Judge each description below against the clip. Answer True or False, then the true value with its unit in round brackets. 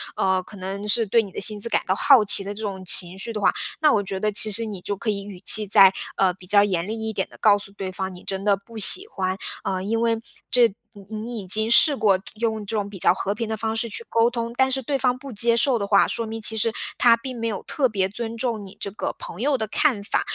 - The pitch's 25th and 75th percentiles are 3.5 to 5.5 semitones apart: False (2.8 semitones)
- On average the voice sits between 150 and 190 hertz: False (215 Hz)